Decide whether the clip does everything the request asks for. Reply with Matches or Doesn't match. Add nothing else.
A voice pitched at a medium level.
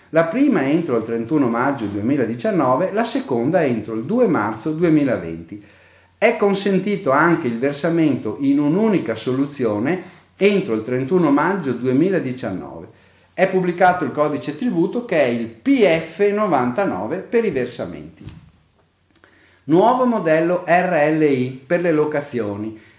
Matches